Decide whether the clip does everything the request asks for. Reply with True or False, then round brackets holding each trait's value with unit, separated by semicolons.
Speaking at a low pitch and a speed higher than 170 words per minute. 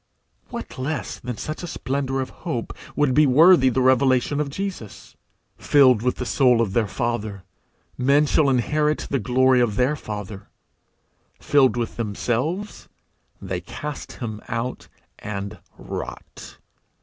False (130 Hz; 135 wpm)